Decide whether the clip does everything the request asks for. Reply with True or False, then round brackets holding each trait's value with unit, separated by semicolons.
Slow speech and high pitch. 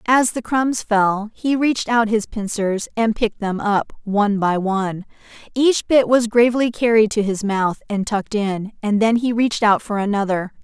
False (190 wpm; 215 Hz)